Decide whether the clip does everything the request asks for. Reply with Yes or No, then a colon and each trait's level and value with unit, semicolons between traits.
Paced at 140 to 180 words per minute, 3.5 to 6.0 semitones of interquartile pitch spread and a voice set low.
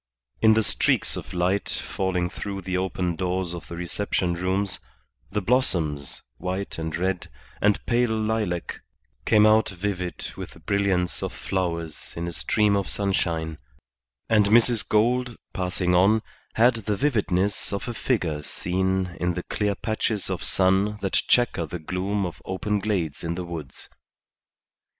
No: average, 150 wpm; average, 3.0 semitones; very low, 95 Hz